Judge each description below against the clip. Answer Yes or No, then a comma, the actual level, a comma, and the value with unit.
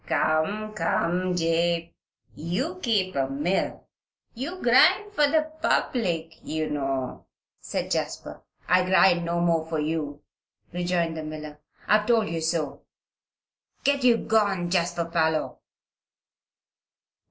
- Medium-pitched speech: Yes, medium, 175 Hz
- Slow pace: Yes, slow, 120 wpm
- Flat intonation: No, average, 5.0 semitones